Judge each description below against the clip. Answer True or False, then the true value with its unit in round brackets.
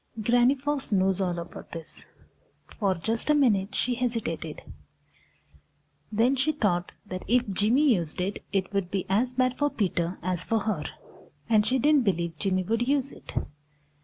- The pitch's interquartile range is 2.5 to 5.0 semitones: False (5.4 semitones)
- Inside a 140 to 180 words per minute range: True (160 wpm)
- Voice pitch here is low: False (210 Hz)